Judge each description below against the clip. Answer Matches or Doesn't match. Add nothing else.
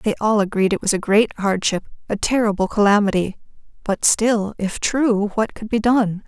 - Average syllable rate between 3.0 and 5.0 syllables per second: Matches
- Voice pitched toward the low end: Doesn't match